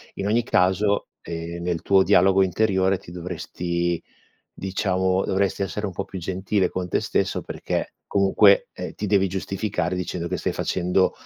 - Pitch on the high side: No, very low, 95 Hz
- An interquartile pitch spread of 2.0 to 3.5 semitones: No, narrow, 1.6 semitones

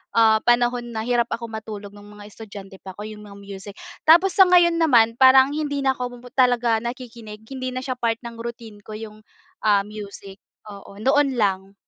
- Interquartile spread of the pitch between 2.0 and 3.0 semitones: No, average, 3.4 semitones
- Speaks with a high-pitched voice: Yes, high, 225 Hz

